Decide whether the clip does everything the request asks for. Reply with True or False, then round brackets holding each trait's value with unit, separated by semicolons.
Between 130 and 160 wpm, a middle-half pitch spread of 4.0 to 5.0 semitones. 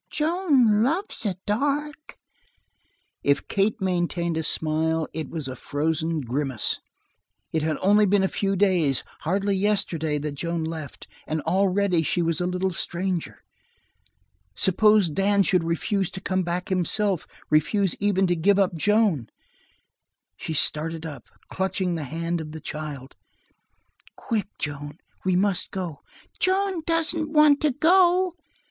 True (140 wpm; 4.4 semitones)